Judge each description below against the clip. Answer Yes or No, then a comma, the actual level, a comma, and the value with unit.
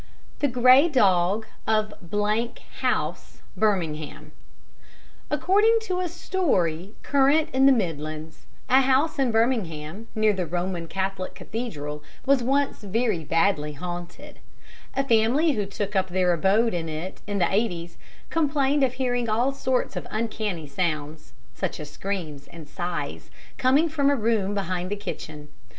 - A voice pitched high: Yes, high, 205 Hz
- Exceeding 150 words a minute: No, average, 140 wpm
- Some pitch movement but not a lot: No, wide, 7.2 semitones